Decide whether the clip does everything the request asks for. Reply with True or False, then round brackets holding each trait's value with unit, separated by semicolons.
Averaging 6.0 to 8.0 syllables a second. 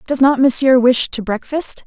False (4.6 syllables/s)